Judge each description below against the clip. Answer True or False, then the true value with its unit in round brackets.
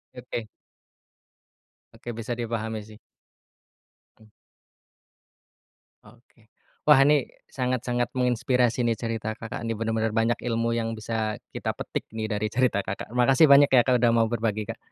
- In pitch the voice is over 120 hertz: False (115 Hz)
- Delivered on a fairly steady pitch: True (1.8 semitones)